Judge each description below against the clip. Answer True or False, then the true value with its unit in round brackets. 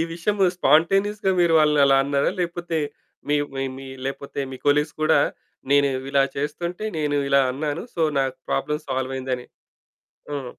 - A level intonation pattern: False (3.7 semitones)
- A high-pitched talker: False (145 Hz)